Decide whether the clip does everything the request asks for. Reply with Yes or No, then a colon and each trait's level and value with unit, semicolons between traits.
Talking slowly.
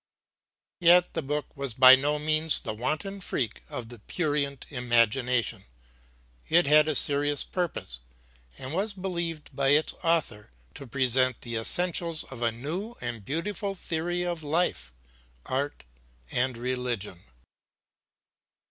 Yes: slow, 130 wpm